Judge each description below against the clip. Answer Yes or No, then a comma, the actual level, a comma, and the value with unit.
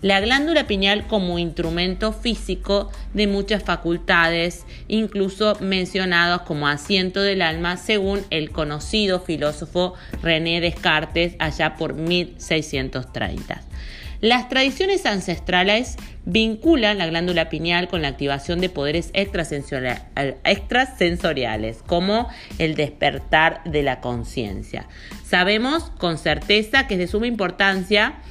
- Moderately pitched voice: Yes, medium, 175 Hz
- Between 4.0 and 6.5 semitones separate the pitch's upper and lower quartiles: Yes, average, 4.3 semitones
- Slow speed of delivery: Yes, slow, 110 wpm